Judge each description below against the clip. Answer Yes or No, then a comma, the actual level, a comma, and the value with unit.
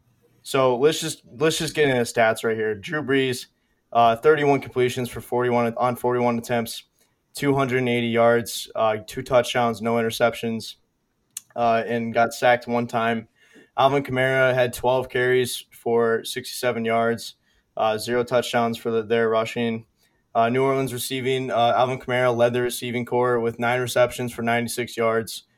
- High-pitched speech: No, low, 120 Hz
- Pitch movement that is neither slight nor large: No, narrow, 1.5 semitones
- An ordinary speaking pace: Yes, average, 160 wpm